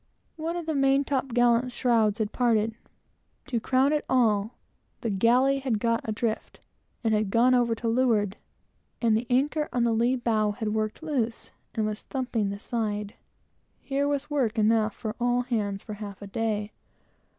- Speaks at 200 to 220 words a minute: No, average, 170 wpm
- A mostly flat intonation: No, average, 3.0 semitones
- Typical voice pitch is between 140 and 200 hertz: No, high, 230 Hz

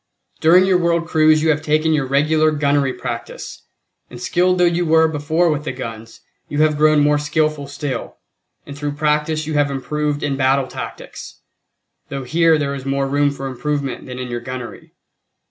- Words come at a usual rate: Yes, average, 180 wpm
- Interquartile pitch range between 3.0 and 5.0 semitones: No, narrow, 2.4 semitones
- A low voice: No, medium, 145 Hz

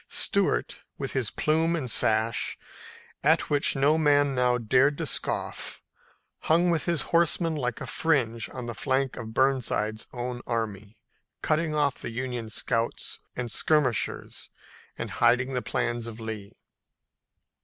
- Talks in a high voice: No, low, 125 Hz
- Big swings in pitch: No, average, 4.1 semitones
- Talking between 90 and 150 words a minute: Yes, average, 140 wpm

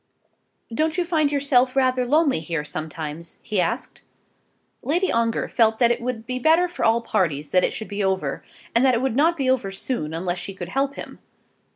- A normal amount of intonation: No, wide, 6.5 semitones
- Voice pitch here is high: Yes, high, 235 Hz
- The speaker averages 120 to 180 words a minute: No, average, 200 wpm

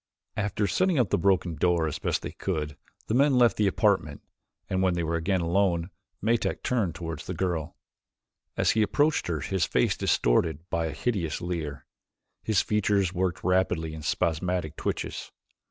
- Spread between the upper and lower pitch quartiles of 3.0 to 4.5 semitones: Yes, average, 3.9 semitones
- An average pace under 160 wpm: No, average, 170 wpm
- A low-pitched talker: Yes, very low, 90 Hz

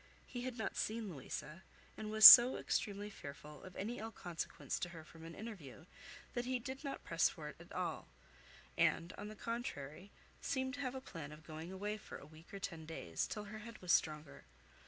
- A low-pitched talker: No, high, 200 Hz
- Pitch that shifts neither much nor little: No, wide, 6.3 semitones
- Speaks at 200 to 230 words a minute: Yes, fast, 205 wpm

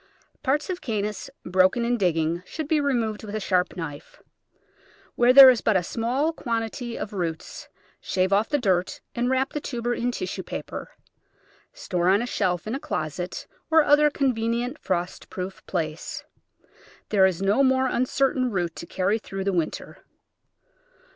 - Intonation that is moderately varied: No, wide, 5.9 semitones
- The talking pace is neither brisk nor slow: Yes, average, 160 wpm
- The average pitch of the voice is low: No, high, 220 Hz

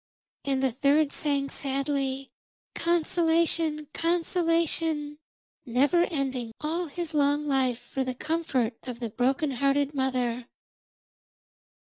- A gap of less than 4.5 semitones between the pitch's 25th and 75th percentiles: Yes, average, 3.5 semitones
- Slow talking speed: Yes, slow, 105 wpm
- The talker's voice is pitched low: No, very high, 280 Hz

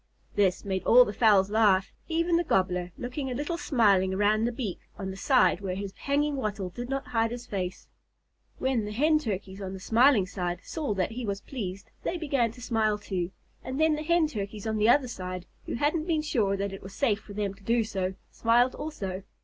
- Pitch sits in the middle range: No, high, 215 Hz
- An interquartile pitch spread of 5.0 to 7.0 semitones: Yes, average, 5.3 semitones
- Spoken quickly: Yes, fast, 215 wpm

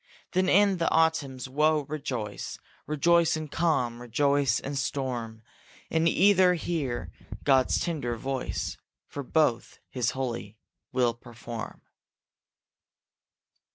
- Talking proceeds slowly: Yes, slow, 105 wpm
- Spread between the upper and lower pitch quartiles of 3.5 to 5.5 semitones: Yes, average, 5.0 semitones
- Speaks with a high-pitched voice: No, low, 135 Hz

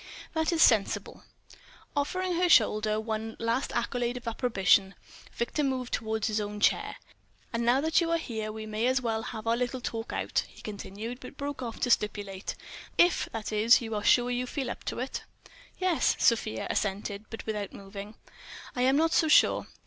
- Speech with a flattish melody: No, average, 3.3 semitones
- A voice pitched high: Yes, high, 230 Hz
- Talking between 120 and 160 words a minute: No, average, 185 wpm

